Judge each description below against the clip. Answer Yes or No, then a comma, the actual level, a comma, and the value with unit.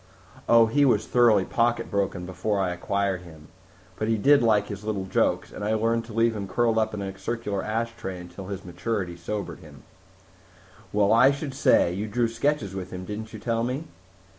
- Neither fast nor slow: Yes, average, 190 wpm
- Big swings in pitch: No, average, 3.2 semitones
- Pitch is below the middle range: Yes, low, 105 Hz